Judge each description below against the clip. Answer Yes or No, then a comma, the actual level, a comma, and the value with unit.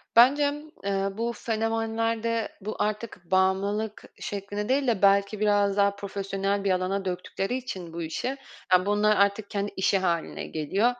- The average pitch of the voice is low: No, high, 200 Hz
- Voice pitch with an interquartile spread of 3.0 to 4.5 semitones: No, narrow, 2.4 semitones